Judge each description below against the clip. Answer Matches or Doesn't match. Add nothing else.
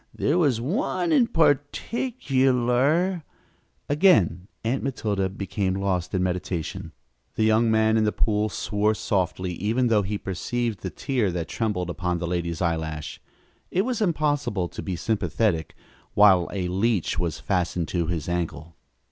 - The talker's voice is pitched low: Matches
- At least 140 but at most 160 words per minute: Matches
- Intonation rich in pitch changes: Matches